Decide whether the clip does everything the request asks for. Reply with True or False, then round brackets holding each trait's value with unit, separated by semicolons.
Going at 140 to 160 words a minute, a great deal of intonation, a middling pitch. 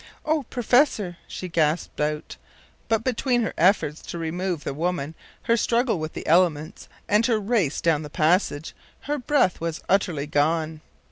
True (155 wpm; 6.3 semitones; 175 Hz)